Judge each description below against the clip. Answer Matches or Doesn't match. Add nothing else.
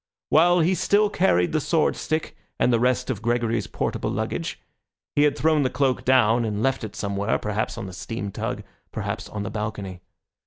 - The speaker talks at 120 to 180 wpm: Doesn't match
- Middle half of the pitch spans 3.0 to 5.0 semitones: Doesn't match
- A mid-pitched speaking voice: Doesn't match